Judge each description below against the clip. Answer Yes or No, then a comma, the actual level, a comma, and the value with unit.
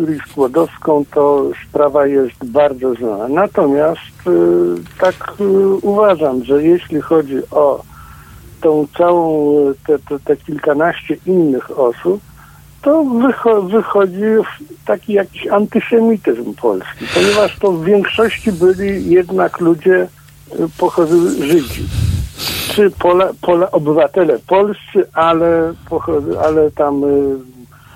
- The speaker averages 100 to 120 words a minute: Yes, slow, 110 wpm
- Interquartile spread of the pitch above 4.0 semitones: Yes, wide, 5.6 semitones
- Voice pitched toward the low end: No, medium, 170 Hz